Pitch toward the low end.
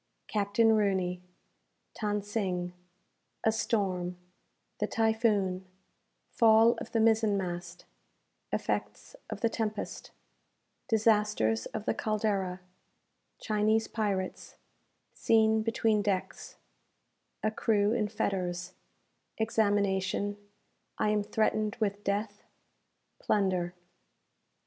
No: high, 210 Hz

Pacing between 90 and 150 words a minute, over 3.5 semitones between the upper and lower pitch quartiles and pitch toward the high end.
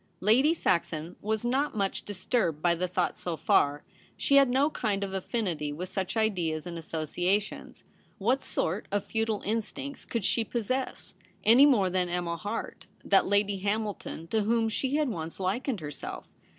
No: average, 170 wpm; average, 4.5 semitones; high, 205 Hz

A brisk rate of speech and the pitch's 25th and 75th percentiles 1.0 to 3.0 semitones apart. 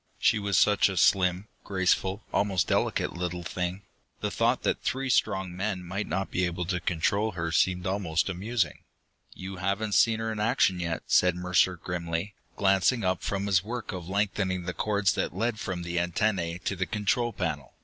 No: average, 180 wpm; narrow, 2.5 semitones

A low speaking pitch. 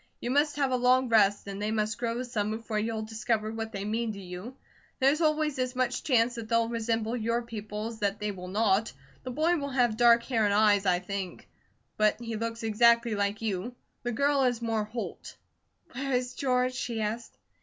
No: high, 230 Hz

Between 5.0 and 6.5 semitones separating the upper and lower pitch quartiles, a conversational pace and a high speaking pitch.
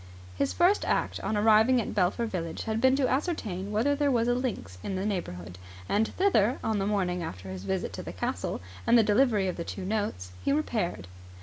No: wide, 5.5 semitones; fast, 210 wpm; high, 210 Hz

